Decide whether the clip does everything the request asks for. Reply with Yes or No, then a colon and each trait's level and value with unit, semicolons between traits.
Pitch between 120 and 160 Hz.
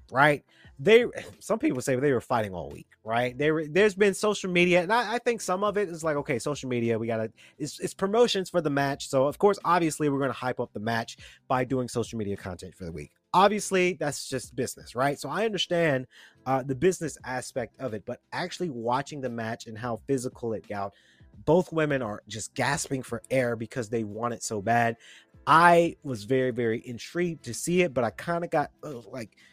Yes: low, 135 Hz